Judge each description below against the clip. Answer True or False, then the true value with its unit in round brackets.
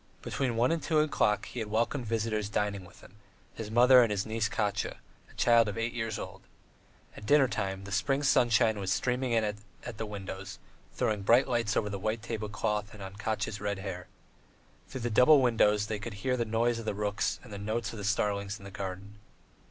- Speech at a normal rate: False (210 wpm)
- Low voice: True (110 Hz)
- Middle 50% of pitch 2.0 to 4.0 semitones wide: True (2.6 semitones)